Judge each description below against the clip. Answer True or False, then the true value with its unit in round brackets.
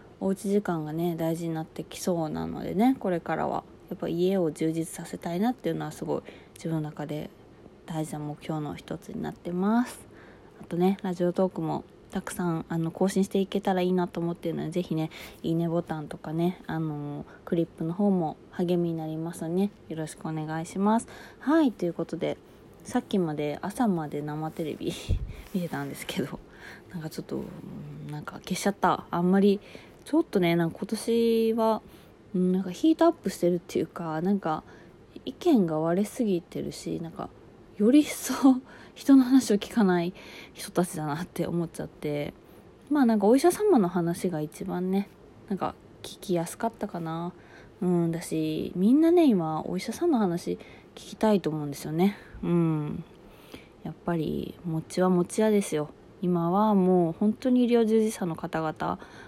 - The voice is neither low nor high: True (180 Hz)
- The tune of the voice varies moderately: True (4.1 semitones)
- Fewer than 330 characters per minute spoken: False (345 characters per minute)